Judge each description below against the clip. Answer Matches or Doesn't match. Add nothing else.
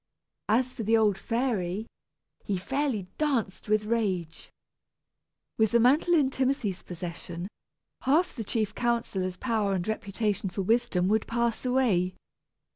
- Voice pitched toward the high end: Matches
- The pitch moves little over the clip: Doesn't match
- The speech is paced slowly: Matches